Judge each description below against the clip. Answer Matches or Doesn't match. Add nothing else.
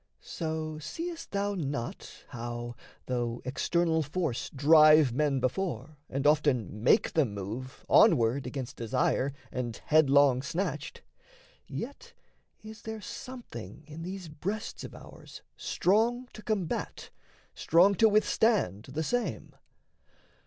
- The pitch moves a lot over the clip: Matches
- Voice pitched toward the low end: Doesn't match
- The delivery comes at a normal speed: Doesn't match